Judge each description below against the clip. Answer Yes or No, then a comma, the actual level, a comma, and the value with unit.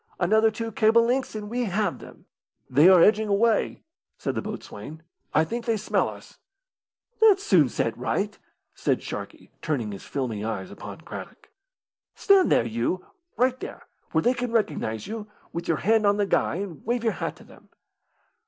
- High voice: Yes, high, 205 Hz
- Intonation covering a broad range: Yes, wide, 6.5 semitones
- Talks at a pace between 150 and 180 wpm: Yes, average, 175 wpm